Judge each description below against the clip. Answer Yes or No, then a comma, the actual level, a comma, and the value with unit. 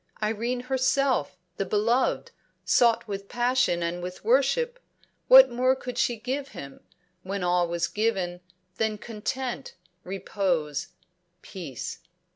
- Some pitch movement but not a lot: No, wide, 5.9 semitones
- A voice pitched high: Yes, high, 220 Hz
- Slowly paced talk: Yes, slow, 115 wpm